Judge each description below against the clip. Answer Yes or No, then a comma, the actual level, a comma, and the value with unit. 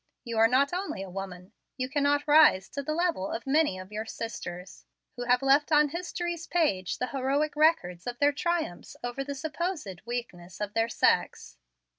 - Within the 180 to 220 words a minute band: Yes, average, 185 wpm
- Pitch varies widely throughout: Yes, wide, 6.6 semitones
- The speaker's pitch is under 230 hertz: No, very high, 265 Hz